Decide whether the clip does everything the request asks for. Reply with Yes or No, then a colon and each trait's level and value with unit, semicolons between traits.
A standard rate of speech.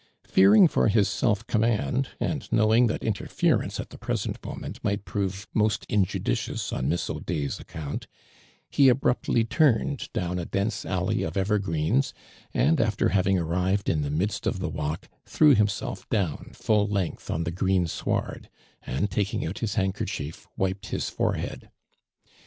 Yes: average, 155 wpm